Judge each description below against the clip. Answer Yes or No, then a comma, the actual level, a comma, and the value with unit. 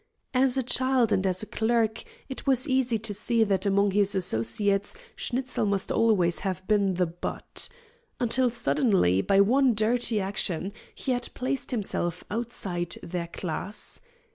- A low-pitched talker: No, high, 210 Hz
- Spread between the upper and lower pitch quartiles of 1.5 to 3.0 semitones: No, average, 4.3 semitones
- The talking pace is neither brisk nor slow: Yes, average, 150 wpm